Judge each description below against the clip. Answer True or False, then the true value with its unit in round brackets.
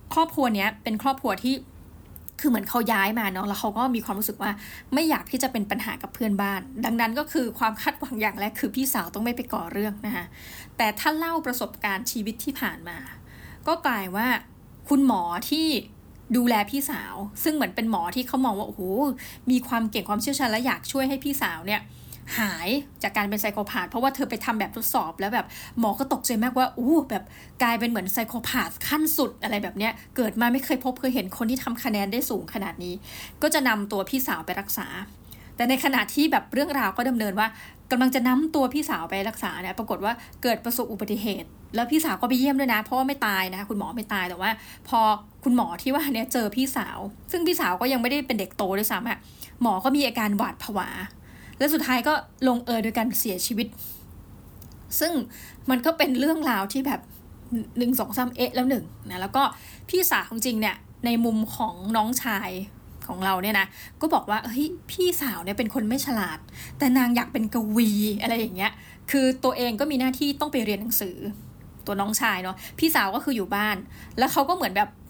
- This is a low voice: False (240 Hz)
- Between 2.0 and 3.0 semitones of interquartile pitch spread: False (4.0 semitones)